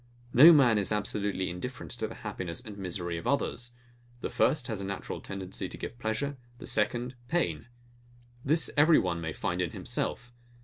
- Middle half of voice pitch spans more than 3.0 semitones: Yes, average, 4.8 semitones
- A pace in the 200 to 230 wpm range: No, average, 175 wpm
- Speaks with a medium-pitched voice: No, low, 110 Hz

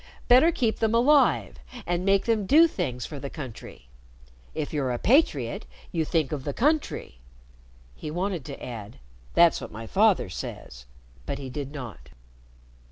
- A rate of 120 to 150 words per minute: No, average, 160 wpm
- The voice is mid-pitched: Yes, medium, 155 Hz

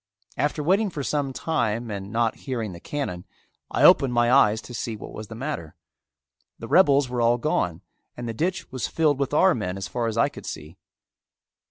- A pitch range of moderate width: Yes, average, 5.0 semitones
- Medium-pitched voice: No, low, 120 Hz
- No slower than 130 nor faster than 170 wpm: No, average, 200 wpm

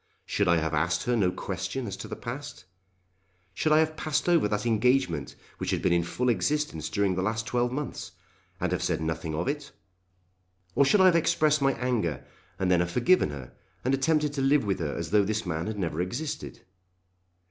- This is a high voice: No, low, 110 Hz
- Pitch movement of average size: No, wide, 8.4 semitones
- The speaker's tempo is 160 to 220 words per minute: Yes, fast, 205 wpm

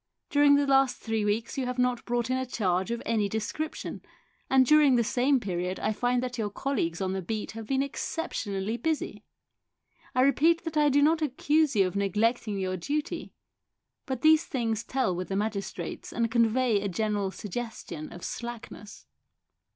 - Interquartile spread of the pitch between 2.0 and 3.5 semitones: No, average, 4.7 semitones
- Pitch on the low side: No, high, 235 Hz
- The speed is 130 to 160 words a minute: No, average, 175 wpm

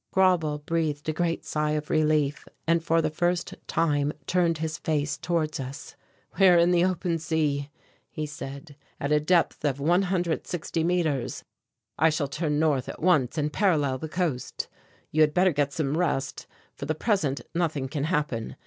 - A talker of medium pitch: Yes, medium, 155 Hz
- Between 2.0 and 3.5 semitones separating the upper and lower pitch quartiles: Yes, average, 2.7 semitones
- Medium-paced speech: Yes, average, 170 wpm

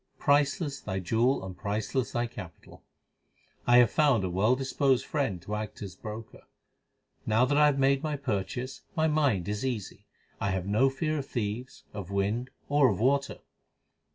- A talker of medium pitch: No, low, 120 Hz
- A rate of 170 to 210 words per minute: Yes, average, 175 wpm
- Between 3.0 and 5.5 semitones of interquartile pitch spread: Yes, average, 5.1 semitones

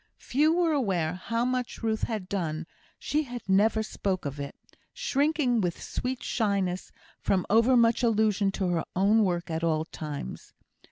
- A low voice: No, high, 210 Hz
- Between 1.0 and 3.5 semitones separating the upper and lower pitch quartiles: No, wide, 5.4 semitones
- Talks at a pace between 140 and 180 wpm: Yes, average, 155 wpm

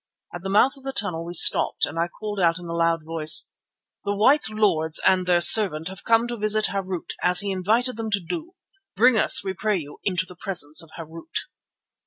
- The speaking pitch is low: No, high, 190 Hz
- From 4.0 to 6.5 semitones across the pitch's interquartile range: Yes, average, 4.3 semitones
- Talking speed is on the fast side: Yes, fast, 215 wpm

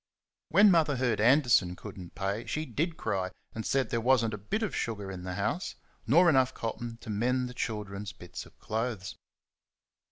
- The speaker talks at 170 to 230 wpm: Yes, average, 190 wpm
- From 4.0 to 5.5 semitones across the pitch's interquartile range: Yes, average, 4.5 semitones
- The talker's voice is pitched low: Yes, low, 115 Hz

